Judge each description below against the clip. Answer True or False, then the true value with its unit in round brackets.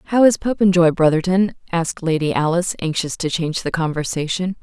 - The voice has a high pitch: False (175 Hz)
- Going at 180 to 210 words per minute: False (155 wpm)